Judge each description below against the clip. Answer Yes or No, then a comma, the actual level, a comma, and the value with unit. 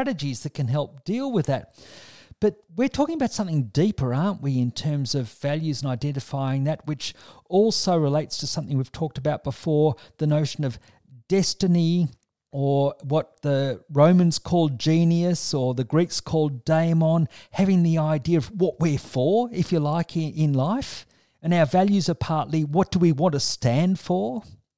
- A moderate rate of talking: Yes, average, 165 wpm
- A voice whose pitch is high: No, medium, 155 Hz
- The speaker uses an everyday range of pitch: Yes, average, 3.9 semitones